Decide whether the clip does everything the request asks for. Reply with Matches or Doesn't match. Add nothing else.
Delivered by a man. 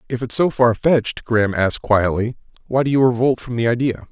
Matches